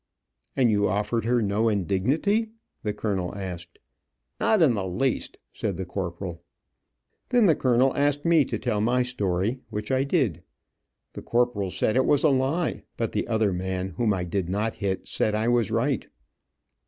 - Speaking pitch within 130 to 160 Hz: No, low, 110 Hz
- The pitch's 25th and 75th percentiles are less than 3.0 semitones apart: No, average, 5.3 semitones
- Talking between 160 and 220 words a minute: Yes, average, 170 wpm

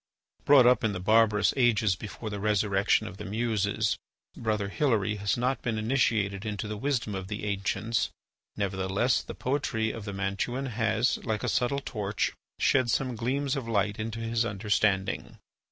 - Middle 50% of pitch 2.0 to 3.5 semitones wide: Yes, average, 2.8 semitones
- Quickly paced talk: No, average, 165 wpm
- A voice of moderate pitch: No, low, 110 Hz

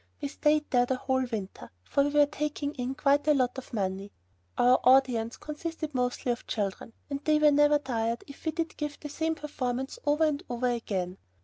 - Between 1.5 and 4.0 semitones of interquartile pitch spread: Yes, average, 3.4 semitones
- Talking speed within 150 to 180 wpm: No, average, 200 wpm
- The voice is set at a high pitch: Yes, very high, 270 Hz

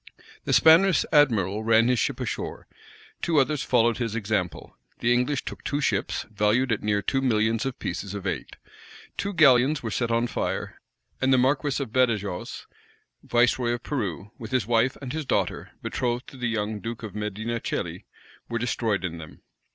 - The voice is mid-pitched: No, low, 120 Hz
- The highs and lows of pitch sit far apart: No, average, 3.6 semitones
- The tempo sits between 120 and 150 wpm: No, average, 175 wpm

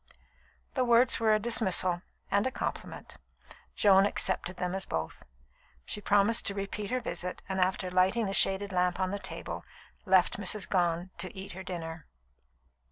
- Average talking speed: Yes, average, 165 wpm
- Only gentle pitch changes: Yes, narrow, 2.2 semitones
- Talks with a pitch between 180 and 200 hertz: Yes, high, 190 Hz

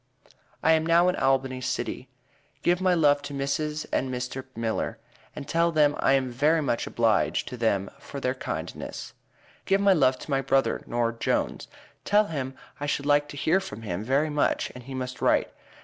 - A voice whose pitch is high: No, medium, 140 Hz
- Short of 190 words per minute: No, average, 195 wpm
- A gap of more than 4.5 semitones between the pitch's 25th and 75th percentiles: No, average, 3.5 semitones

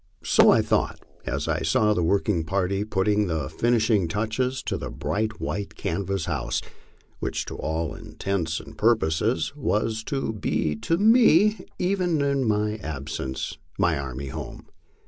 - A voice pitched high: No, low, 100 Hz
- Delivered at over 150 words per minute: No, average, 145 wpm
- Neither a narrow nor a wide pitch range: No, wide, 6.5 semitones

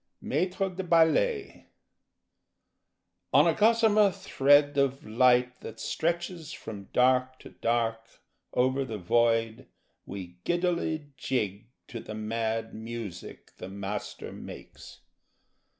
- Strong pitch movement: Yes, wide, 6.9 semitones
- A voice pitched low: Yes, low, 125 Hz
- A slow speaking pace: Yes, slow, 105 wpm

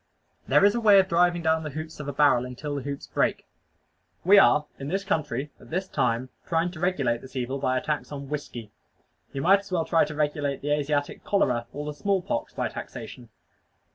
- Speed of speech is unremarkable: No, fast, 215 wpm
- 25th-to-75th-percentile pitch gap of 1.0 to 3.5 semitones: No, average, 4.2 semitones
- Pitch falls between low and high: Yes, medium, 150 Hz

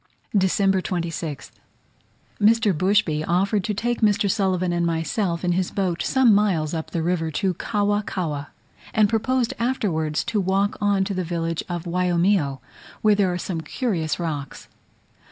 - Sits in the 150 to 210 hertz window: Yes, medium, 185 Hz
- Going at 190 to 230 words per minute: No, average, 155 wpm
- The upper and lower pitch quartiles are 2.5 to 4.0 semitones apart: Yes, average, 3.5 semitones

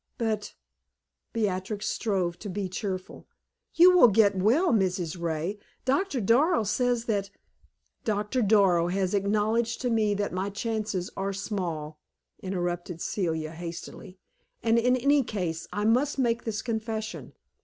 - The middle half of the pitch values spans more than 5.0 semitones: No, average, 3.7 semitones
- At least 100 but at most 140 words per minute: Yes, slow, 135 wpm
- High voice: Yes, high, 205 Hz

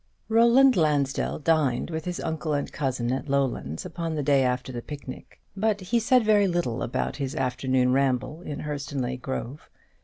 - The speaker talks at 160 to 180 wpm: Yes, average, 165 wpm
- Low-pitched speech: No, medium, 145 Hz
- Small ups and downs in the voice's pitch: No, average, 4.8 semitones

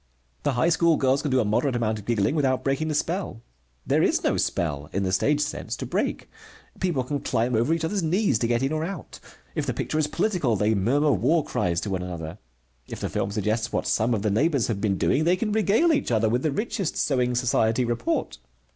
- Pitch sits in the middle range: No, low, 130 Hz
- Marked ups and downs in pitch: Yes, wide, 6.2 semitones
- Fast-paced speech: Yes, fast, 230 wpm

